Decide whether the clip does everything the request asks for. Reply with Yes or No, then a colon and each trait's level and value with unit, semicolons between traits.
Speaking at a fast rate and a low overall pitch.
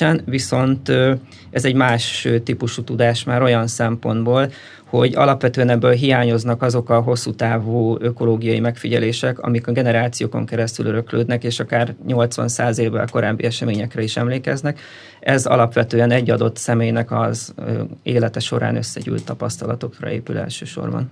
No: average, 125 wpm; low, 120 Hz